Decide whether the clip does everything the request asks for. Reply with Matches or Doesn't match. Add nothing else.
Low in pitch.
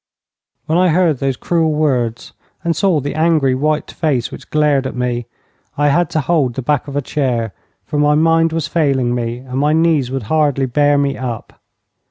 Doesn't match